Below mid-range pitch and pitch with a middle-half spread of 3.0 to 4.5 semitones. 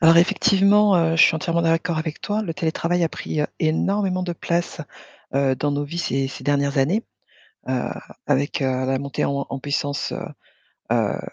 No: medium, 160 Hz; average, 3.7 semitones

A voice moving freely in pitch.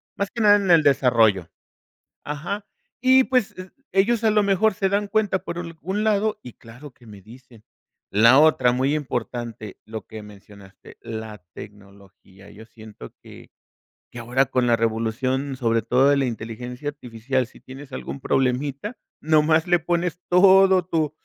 Yes: wide, 8.0 semitones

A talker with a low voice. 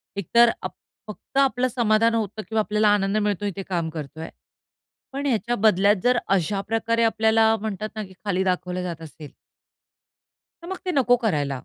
No: high, 210 Hz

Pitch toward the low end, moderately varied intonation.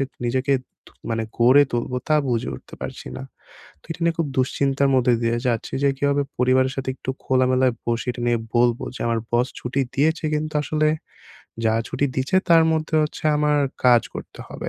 Yes: low, 130 Hz; average, 3.3 semitones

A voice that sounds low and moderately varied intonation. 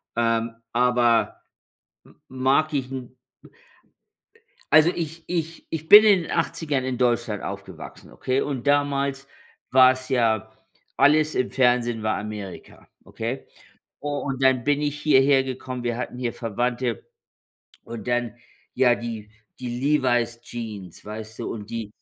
Yes: low, 125 Hz; average, 3.2 semitones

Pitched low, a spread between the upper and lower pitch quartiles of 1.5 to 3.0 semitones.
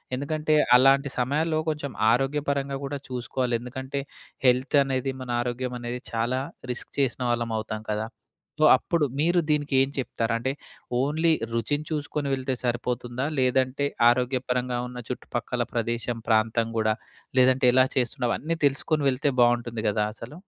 Yes: low, 130 Hz; average, 2.7 semitones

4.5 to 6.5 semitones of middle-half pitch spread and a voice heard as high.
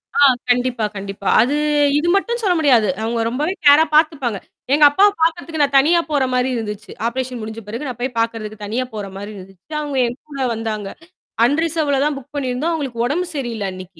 Yes: average, 5.0 semitones; very high, 255 Hz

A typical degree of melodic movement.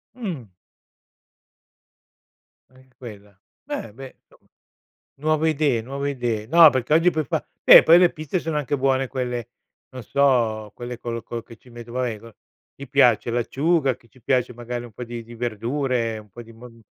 Yes: average, 3.2 semitones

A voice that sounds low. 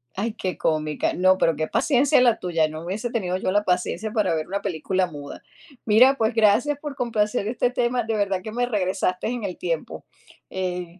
No: high, 200 Hz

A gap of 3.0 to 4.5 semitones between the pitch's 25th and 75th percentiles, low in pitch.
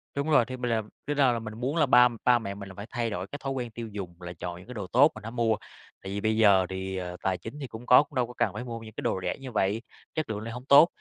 Yes: average, 4.2 semitones; low, 115 Hz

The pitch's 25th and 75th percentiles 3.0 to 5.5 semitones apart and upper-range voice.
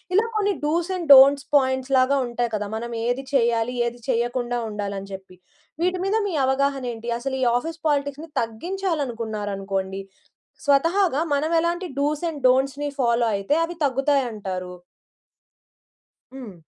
Yes: average, 4.3 semitones; very high, 265 Hz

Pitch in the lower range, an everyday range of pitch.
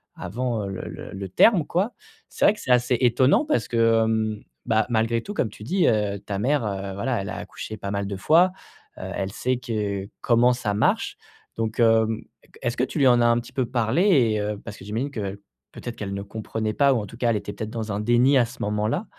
Yes: low, 115 Hz; average, 3.2 semitones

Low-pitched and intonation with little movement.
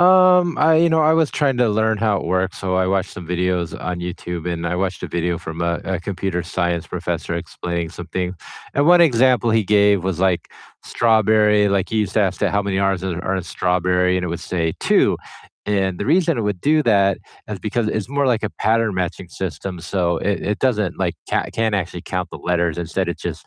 No: very low, 95 Hz; average, 3.7 semitones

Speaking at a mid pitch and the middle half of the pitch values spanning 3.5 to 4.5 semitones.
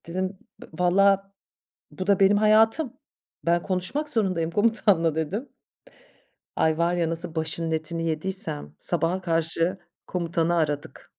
No: medium, 175 Hz; average, 3.1 semitones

